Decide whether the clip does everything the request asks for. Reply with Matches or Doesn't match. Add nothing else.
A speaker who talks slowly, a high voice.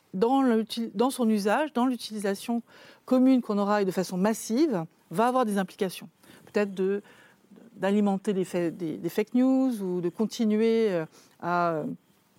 Matches